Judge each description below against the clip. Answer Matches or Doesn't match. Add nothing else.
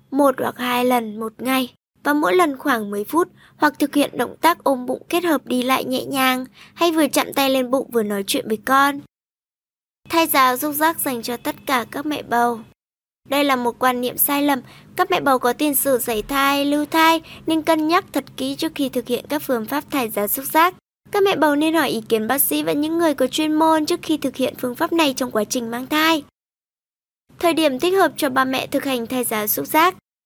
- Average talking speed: Matches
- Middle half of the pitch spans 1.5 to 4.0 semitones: Matches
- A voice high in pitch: Matches